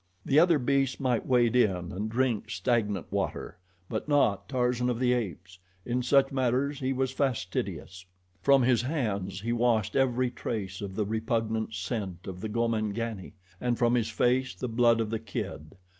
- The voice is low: Yes, low, 120 Hz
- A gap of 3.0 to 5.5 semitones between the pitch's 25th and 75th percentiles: Yes, average, 3.3 semitones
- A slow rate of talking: No, average, 170 wpm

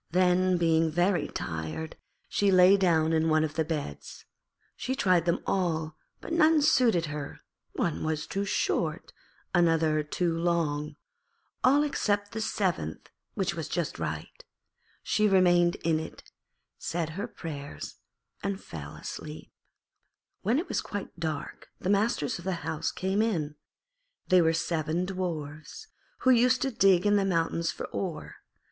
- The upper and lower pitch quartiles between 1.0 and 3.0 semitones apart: No, average, 3.8 semitones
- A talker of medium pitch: Yes, medium, 175 Hz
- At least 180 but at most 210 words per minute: No, average, 145 wpm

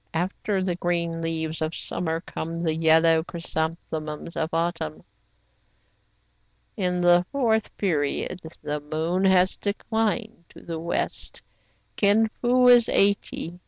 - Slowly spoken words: Yes, slow, 120 wpm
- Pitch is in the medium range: Yes, medium, 170 Hz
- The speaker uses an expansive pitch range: No, average, 3.7 semitones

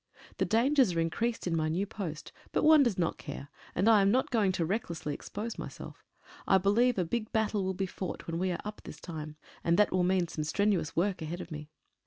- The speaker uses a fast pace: Yes, fast, 235 wpm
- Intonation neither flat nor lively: Yes, average, 4.4 semitones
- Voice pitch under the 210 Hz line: Yes, high, 190 Hz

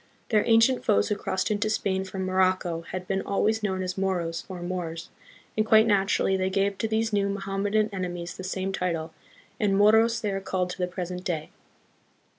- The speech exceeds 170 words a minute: Yes, average, 190 wpm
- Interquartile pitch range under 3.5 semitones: Yes, narrow, 2.4 semitones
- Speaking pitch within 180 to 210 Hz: Yes, high, 190 Hz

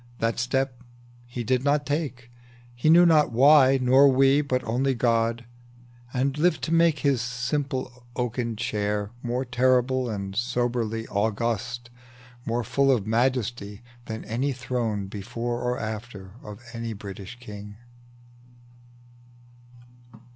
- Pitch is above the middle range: No, low, 120 Hz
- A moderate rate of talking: No, slow, 125 wpm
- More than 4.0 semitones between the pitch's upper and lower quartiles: No, average, 2.8 semitones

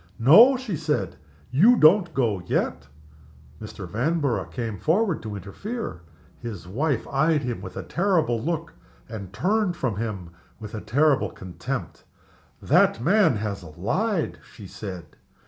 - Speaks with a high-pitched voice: No, low, 125 Hz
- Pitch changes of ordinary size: No, wide, 8.4 semitones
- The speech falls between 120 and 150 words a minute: Yes, slow, 135 wpm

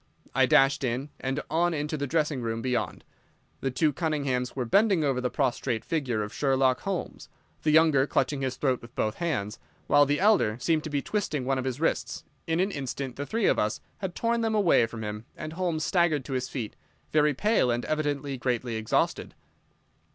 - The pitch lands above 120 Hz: Yes, medium, 140 Hz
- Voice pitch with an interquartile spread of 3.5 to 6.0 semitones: Yes, average, 4.1 semitones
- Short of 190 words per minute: No, average, 195 wpm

